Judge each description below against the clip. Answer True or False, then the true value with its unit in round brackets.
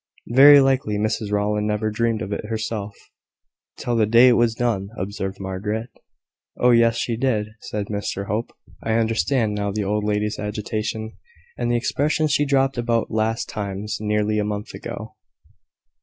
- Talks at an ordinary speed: True (160 wpm)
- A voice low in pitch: True (110 Hz)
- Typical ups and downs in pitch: False (2.1 semitones)